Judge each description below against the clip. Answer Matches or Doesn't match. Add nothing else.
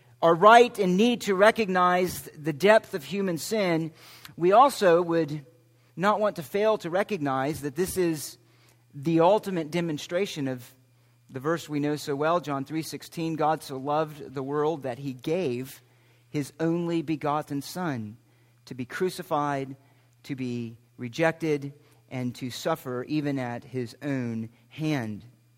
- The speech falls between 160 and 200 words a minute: Doesn't match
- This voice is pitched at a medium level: Matches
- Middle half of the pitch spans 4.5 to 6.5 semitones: Matches